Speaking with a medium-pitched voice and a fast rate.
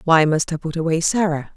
Yes: medium, 165 Hz; fast, 230 wpm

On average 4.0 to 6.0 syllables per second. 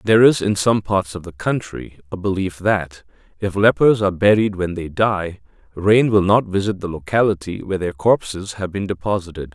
Yes: 5.2 syllables/s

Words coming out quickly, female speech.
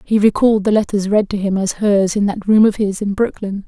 Yes: fast, 260 wpm; female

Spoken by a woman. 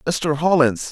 No: male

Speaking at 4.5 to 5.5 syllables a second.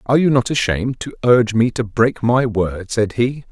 Yes: 5.2 syllables/s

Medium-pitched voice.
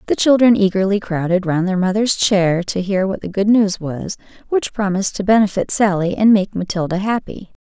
No: high, 195 Hz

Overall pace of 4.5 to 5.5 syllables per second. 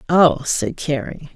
No: 3.6 syllables/s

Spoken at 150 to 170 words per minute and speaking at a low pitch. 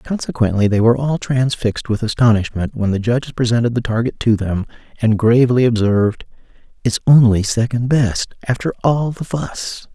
Yes: average, 155 wpm; low, 115 Hz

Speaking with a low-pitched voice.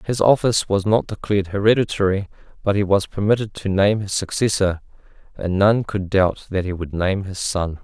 Yes: low, 100 Hz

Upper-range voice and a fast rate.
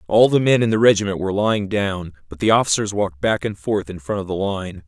No: low, 100 Hz; fast, 260 wpm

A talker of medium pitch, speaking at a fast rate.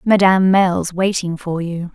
No: medium, 180 Hz; average, 155 wpm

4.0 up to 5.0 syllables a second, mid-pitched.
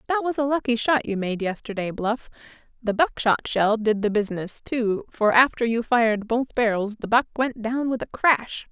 No: 4.9 syllables/s; high, 235 Hz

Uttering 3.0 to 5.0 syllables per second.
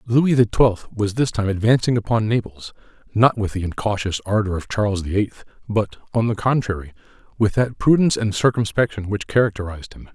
No: 5.6 syllables/s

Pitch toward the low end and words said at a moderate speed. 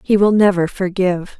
No: high, 190 Hz; average, 170 wpm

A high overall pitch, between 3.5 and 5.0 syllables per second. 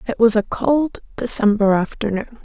Yes: high, 220 Hz; 4.7 syllables/s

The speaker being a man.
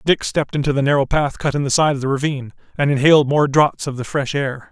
Yes: male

